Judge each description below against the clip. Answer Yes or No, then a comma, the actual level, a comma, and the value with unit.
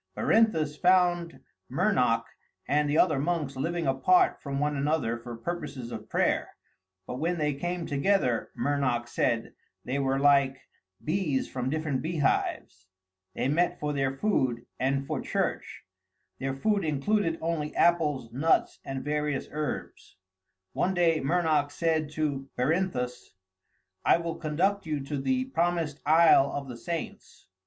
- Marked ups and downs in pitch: No, average, 3.9 semitones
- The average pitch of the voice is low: No, medium, 150 Hz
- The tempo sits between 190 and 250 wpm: No, average, 140 wpm